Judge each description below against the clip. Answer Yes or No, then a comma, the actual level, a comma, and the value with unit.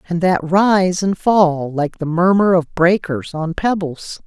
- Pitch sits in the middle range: Yes, medium, 175 Hz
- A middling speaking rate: Yes, average, 170 wpm